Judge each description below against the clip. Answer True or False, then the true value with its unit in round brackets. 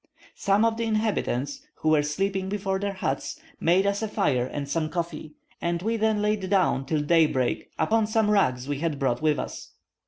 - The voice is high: False (180 Hz)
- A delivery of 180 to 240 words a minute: True (190 wpm)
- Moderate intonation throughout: False (5.9 semitones)